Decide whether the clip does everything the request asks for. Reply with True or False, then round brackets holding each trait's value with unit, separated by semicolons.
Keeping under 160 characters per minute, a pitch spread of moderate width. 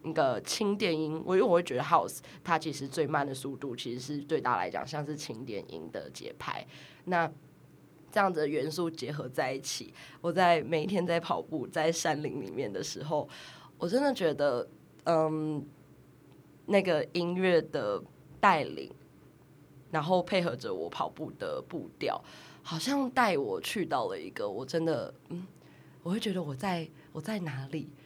False (245 characters per minute; 3.5 semitones)